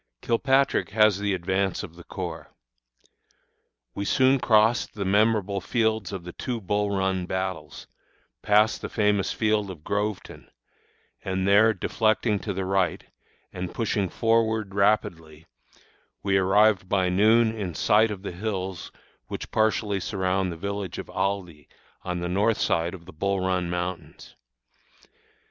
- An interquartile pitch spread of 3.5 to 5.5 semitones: No, average, 2.7 semitones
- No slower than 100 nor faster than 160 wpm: Yes, average, 140 wpm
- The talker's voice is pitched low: Yes, low, 100 Hz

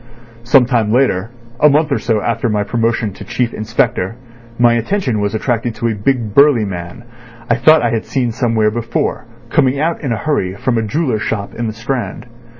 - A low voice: Yes, low, 115 Hz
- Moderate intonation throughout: Yes, average, 3.1 semitones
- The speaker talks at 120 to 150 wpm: No, average, 195 wpm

